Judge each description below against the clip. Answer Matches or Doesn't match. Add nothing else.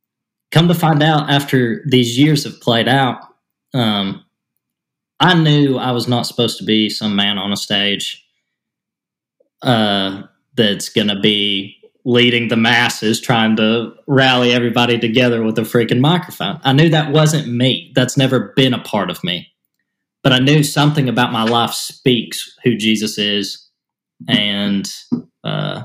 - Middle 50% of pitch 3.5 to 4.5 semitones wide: Matches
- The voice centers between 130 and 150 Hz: Doesn't match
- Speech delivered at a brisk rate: Doesn't match